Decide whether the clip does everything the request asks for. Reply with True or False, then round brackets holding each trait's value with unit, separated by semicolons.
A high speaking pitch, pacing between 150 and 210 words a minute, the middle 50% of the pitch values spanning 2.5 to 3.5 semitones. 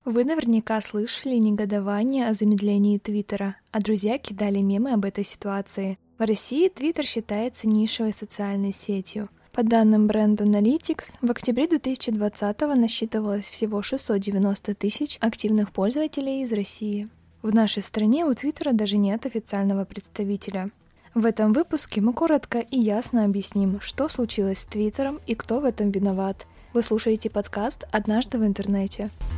False (215 Hz; 140 wpm; 2.8 semitones)